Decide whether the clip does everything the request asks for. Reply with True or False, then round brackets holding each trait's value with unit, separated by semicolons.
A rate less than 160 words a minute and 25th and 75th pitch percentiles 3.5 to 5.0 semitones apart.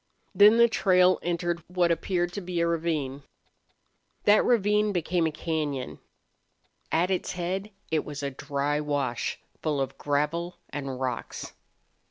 True (140 wpm; 3.9 semitones)